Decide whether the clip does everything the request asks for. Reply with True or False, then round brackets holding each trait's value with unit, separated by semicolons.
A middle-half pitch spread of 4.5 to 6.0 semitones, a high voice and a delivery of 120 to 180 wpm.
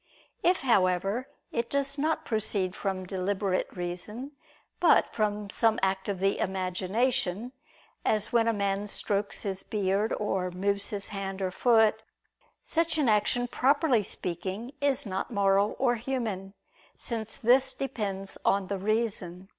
False (3.7 semitones; 205 Hz; 140 wpm)